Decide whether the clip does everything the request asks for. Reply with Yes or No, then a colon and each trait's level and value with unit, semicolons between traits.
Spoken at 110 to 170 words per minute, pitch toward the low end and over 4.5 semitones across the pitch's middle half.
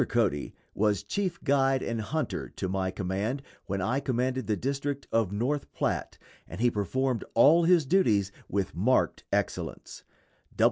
Yes: average, 145 wpm; low, 120 Hz; wide, 5.4 semitones